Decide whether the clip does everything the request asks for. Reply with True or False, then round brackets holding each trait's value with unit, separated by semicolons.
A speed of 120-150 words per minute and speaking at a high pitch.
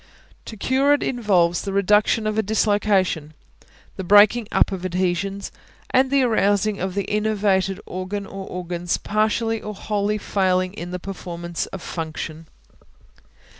True (140 wpm; 200 Hz)